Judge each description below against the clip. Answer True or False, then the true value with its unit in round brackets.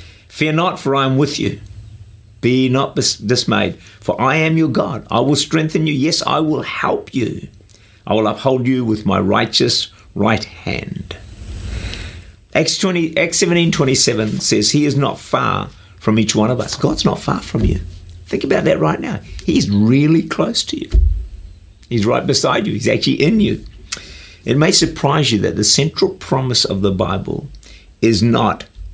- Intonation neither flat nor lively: False (6.0 semitones)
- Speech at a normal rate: True (175 wpm)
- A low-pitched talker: True (110 Hz)